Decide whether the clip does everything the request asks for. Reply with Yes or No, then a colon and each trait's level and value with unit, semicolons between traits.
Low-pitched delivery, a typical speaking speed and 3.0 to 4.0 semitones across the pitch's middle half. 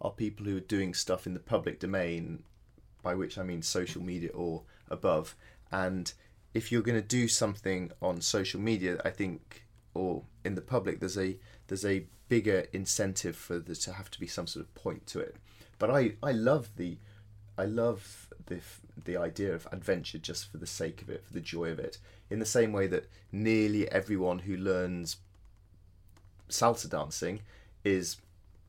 No: very low, 95 Hz; average, 180 wpm; narrow, 2.5 semitones